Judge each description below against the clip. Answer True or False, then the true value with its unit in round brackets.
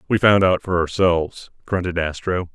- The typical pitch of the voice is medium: False (90 Hz)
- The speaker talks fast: False (165 wpm)